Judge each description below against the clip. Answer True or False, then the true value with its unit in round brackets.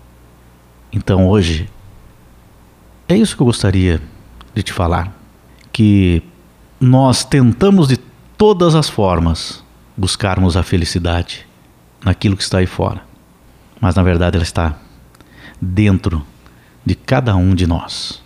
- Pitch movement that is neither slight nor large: True (4.4 semitones)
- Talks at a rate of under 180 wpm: True (120 wpm)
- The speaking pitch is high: False (95 Hz)